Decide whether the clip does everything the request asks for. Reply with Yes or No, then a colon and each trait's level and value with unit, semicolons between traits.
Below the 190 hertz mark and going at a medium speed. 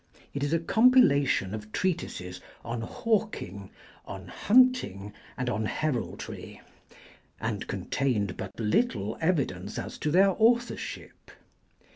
No: medium, 140 Hz; slow, 110 wpm